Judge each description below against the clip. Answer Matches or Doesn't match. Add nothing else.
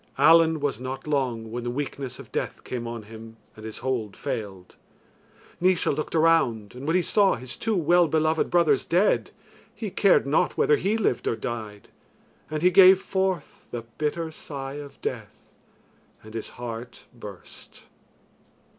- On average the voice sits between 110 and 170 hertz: Matches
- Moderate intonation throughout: Doesn't match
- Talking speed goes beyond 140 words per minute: Matches